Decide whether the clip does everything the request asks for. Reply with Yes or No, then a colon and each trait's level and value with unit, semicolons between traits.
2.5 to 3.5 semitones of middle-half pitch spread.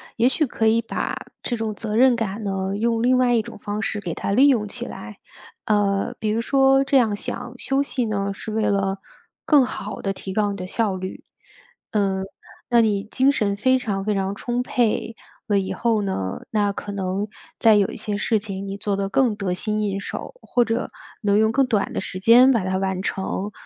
Yes: average, 2.9 semitones